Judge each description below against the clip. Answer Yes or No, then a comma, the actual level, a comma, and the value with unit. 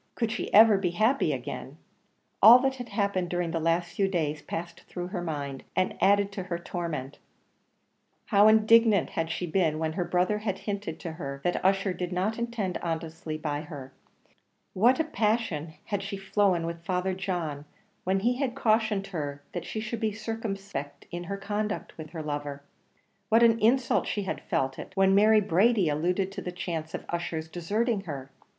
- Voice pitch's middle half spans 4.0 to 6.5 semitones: Yes, average, 4.4 semitones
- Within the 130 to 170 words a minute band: No, average, 185 wpm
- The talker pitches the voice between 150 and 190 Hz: Yes, medium, 185 Hz